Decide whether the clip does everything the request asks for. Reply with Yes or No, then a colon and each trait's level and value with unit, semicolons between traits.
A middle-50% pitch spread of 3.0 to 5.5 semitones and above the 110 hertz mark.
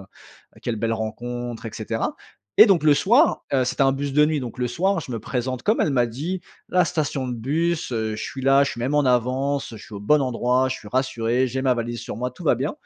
Yes: average, 3.3 semitones; low, 130 Hz